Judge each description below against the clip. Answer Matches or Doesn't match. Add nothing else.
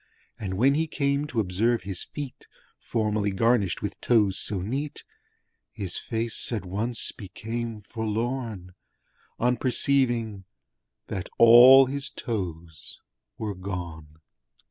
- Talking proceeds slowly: Matches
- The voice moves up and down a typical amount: Matches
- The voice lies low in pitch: Matches